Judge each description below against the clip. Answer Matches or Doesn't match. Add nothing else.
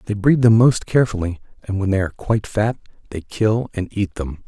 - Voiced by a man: Matches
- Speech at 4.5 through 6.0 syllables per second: Matches